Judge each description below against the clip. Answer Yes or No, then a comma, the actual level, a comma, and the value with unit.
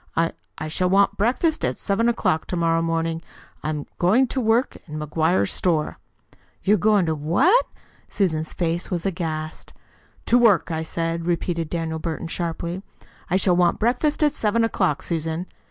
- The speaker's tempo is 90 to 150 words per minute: No, average, 170 wpm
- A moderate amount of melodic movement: Yes, average, 4.1 semitones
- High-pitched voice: No, medium, 170 Hz